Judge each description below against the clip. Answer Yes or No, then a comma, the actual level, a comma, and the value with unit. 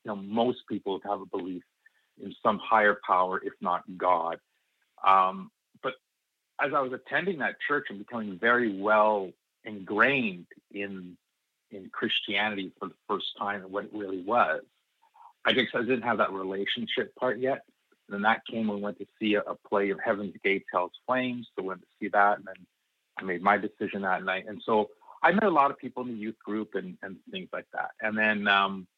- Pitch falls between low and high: No, low, 105 Hz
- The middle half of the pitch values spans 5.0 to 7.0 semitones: No, narrow, 2.5 semitones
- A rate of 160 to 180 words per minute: No, fast, 205 wpm